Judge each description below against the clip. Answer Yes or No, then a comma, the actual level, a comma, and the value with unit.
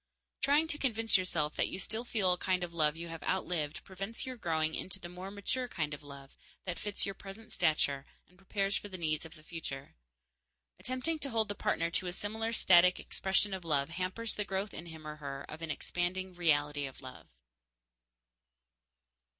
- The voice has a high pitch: No, medium, 180 Hz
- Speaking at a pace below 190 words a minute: No, average, 195 wpm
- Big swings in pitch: No, average, 4.5 semitones